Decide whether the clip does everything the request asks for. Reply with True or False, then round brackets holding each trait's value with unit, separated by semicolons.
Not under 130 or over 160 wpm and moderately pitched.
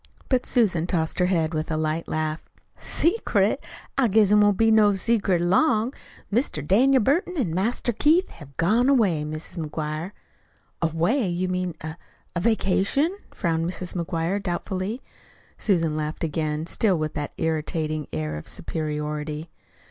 True (150 wpm; 175 Hz)